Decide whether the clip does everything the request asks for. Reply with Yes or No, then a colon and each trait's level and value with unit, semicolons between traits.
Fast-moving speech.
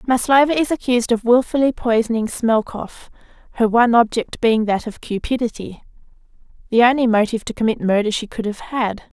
No: average, 155 wpm